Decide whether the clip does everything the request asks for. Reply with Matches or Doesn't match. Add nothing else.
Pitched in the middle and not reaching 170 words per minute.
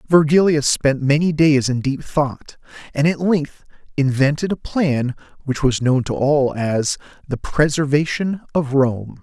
Matches